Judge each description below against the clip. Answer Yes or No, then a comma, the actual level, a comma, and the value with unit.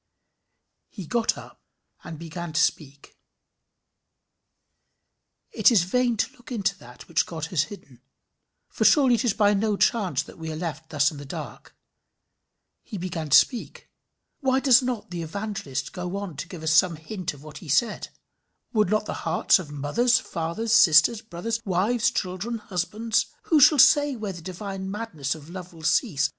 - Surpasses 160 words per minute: Yes, average, 175 wpm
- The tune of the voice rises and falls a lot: Yes, wide, 5.8 semitones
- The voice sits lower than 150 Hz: No, medium, 185 Hz